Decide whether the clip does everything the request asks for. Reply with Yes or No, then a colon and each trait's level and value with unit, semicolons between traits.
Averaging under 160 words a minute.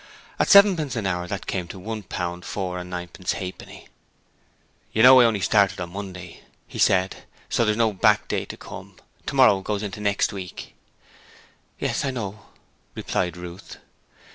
No: average, 165 wpm